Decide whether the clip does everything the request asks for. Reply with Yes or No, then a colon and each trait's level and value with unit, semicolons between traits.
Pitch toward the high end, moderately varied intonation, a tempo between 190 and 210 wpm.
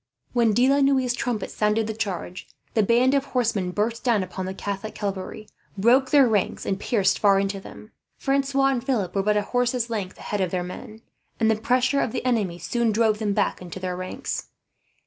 Yes: high, 220 Hz; average, 4.0 semitones; fast, 205 wpm